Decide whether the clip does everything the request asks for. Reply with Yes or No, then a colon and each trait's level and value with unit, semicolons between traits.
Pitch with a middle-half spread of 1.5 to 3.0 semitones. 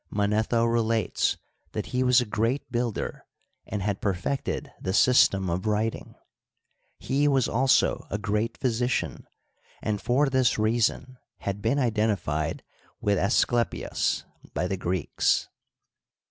No: average, 3.4 semitones